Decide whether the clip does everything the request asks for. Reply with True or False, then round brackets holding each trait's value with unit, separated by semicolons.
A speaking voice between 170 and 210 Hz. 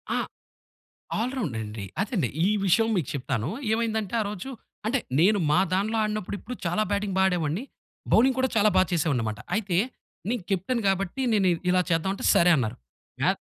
True (195 Hz)